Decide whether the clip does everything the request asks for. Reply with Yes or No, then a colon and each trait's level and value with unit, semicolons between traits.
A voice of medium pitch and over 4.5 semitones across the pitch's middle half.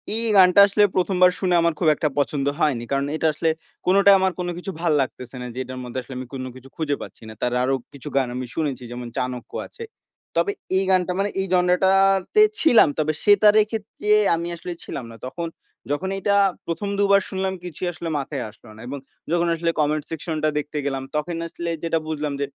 Yes: medium, 165 Hz; wide, 5.5 semitones